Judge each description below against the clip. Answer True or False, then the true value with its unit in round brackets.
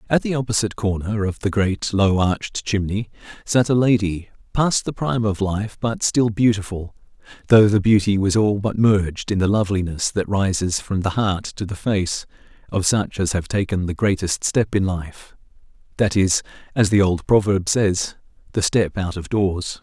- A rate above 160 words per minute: True (180 wpm)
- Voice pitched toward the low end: True (100 Hz)